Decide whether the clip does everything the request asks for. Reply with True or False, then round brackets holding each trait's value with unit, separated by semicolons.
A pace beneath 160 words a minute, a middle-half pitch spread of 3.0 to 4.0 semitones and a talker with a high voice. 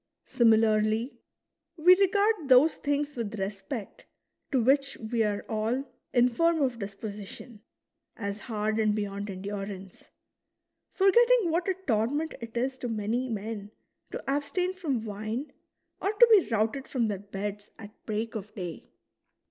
False (140 wpm; 5.3 semitones; 225 Hz)